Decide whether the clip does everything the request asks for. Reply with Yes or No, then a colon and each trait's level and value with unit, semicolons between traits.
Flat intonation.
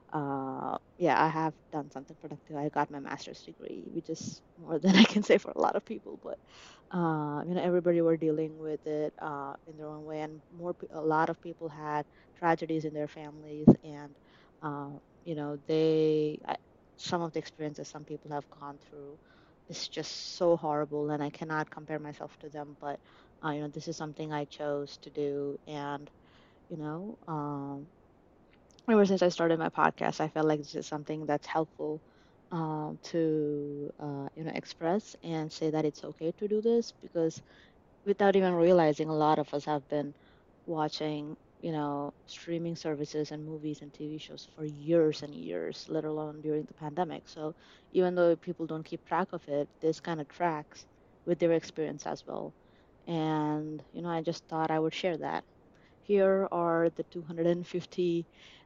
Yes: narrow, 2.0 semitones